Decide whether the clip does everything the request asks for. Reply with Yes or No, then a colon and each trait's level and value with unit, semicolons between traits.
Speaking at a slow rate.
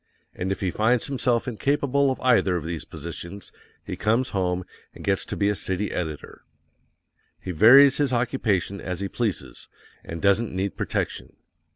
No: average, 165 wpm